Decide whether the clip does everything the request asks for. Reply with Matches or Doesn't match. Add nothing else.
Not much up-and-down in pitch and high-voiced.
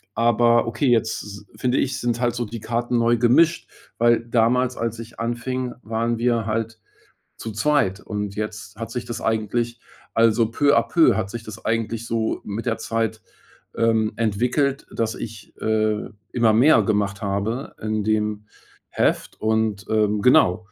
Doesn't match